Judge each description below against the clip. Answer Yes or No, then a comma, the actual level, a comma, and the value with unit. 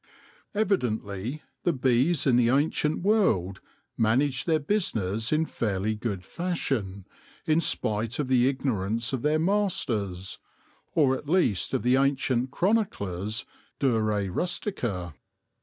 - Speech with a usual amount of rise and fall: No, wide, 6.6 semitones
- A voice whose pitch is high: No, low, 125 Hz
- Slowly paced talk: Yes, slow, 125 wpm